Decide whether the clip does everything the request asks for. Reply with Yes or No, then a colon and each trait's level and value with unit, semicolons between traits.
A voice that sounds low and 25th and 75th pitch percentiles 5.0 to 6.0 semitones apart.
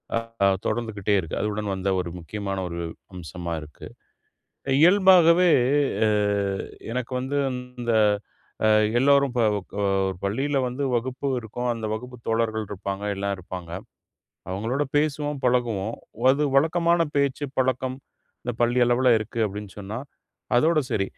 Yes: low, 120 Hz; wide, 5.5 semitones